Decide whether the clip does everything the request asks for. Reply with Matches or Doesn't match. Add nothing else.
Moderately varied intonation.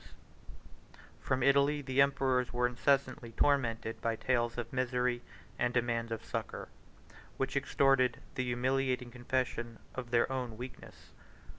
Doesn't match